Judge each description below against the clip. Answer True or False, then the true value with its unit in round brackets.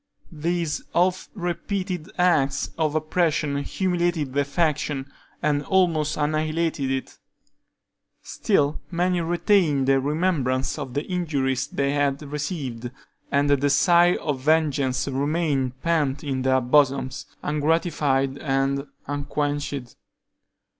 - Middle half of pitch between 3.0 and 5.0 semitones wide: True (3.5 semitones)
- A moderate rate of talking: False (105 wpm)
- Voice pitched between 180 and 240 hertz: False (145 Hz)